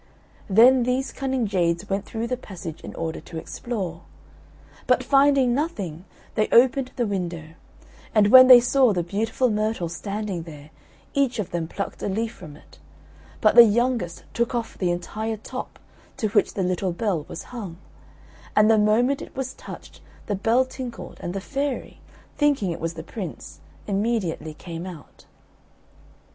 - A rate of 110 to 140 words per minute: No, average, 160 wpm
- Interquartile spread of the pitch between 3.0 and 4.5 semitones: No, wide, 5.6 semitones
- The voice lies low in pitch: No, high, 210 Hz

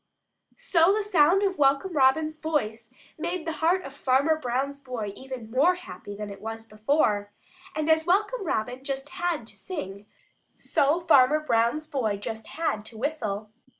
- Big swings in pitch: Yes, wide, 6.2 semitones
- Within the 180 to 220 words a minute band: No, average, 160 wpm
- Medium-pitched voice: No, very high, 275 Hz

